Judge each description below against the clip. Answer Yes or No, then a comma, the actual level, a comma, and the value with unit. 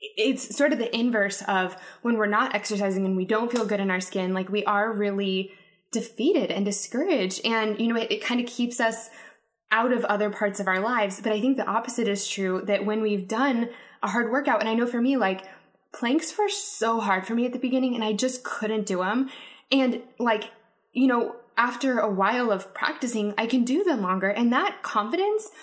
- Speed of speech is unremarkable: No, fast, 220 wpm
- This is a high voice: Yes, high, 225 Hz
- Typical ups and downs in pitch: Yes, average, 3.8 semitones